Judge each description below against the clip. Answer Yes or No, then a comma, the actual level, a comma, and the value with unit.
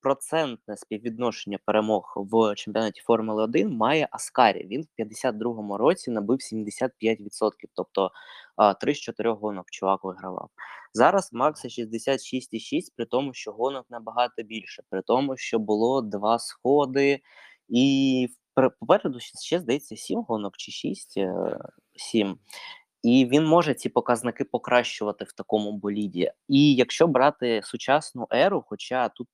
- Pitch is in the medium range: No, low, 115 Hz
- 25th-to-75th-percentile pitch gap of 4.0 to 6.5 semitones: No, average, 3.3 semitones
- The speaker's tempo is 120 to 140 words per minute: Yes, average, 125 wpm